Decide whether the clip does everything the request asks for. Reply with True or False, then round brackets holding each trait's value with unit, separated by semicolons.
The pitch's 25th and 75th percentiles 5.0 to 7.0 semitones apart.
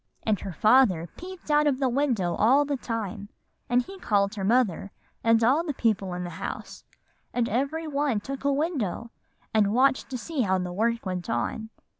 True (5.5 semitones)